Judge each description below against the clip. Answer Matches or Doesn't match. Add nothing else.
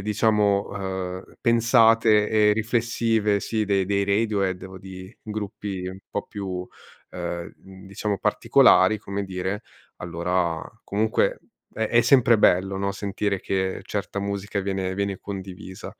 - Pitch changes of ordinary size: Doesn't match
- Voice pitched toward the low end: Matches